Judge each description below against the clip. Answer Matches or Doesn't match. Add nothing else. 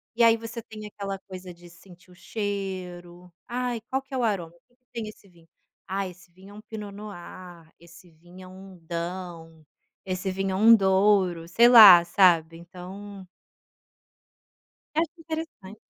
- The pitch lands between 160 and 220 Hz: Matches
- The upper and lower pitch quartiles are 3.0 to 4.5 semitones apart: Matches